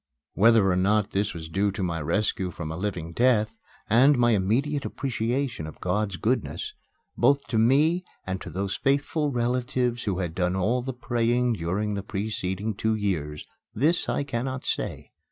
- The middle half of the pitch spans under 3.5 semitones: No, average, 4.9 semitones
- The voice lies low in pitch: Yes, low, 110 Hz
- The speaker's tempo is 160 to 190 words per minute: Yes, average, 170 wpm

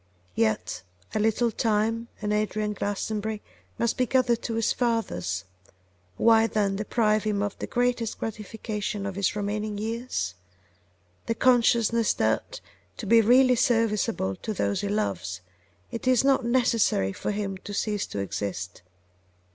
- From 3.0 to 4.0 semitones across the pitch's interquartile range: No, narrow, 2.5 semitones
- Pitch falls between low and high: No, high, 215 Hz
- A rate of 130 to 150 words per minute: Yes, average, 140 wpm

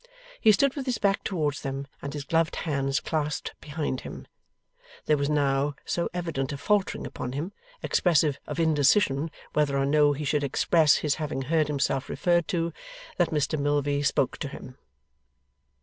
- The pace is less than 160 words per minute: No, average, 165 wpm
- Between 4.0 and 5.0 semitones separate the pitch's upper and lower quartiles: No, average, 2.8 semitones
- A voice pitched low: No, medium, 150 Hz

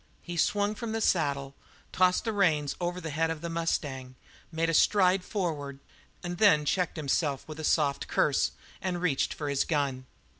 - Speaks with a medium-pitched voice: Yes, medium, 165 Hz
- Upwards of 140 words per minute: Yes, average, 180 wpm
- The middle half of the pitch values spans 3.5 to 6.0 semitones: Yes, average, 4.0 semitones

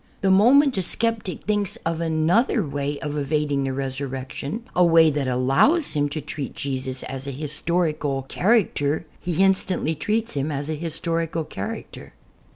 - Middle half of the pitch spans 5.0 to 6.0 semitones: Yes, average, 5.3 semitones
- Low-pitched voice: No, medium, 155 Hz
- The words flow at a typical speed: Yes, average, 160 wpm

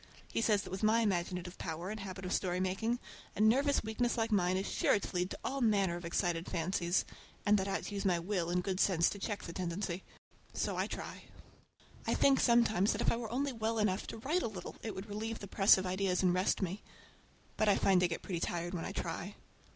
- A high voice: Yes, high, 195 Hz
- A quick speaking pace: Yes, fast, 240 wpm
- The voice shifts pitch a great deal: No, average, 3.3 semitones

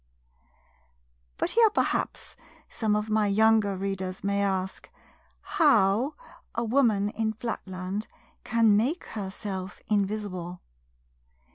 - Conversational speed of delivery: No, slow, 100 wpm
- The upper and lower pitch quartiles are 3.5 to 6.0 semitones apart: No, narrow, 2.5 semitones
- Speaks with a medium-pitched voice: No, high, 210 Hz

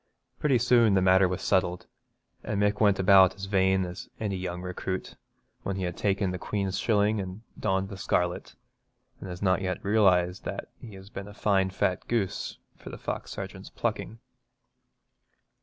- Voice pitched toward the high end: No, very low, 95 Hz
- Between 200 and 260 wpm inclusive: No, average, 175 wpm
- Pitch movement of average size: No, narrow, 1.8 semitones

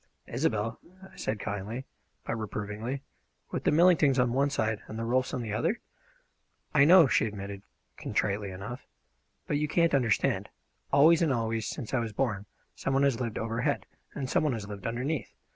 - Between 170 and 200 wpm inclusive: Yes, average, 175 wpm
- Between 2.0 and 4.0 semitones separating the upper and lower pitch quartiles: No, average, 4.6 semitones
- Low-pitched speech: Yes, low, 120 Hz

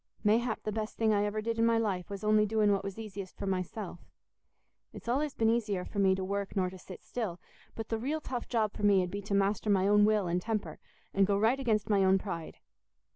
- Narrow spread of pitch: Yes, narrow, 2.3 semitones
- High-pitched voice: Yes, high, 205 Hz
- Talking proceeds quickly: Yes, fast, 240 wpm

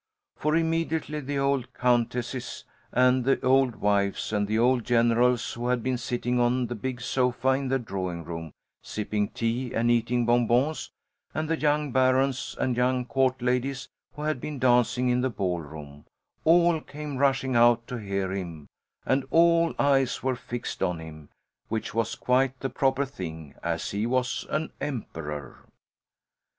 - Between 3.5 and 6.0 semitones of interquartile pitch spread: No, average, 3.0 semitones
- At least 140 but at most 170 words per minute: Yes, average, 160 wpm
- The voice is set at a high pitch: No, low, 125 Hz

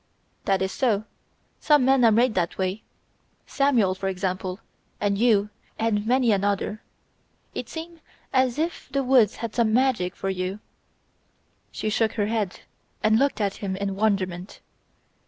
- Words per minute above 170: No, average, 155 wpm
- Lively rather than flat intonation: No, average, 4.3 semitones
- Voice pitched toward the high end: Yes, high, 215 Hz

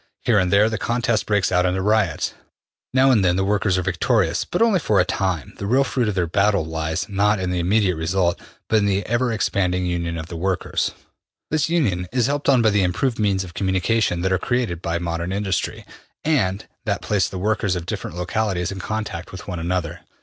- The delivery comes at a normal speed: No, fast, 215 wpm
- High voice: No, very low, 95 Hz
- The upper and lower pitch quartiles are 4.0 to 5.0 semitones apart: No, average, 3.6 semitones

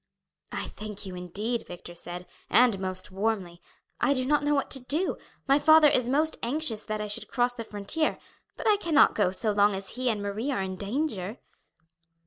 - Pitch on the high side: Yes, high, 220 Hz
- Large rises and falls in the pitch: Yes, wide, 6.0 semitones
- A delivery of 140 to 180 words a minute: No, average, 195 wpm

